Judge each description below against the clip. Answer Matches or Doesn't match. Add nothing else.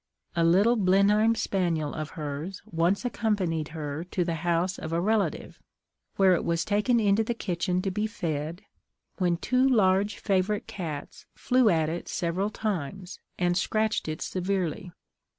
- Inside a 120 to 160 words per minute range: Matches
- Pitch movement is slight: Doesn't match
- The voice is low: Doesn't match